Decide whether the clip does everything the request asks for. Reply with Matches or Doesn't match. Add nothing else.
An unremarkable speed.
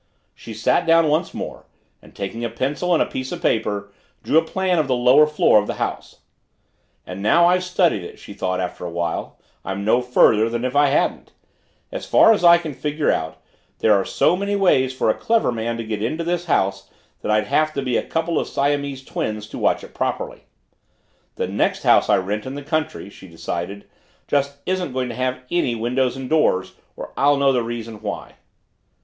Doesn't match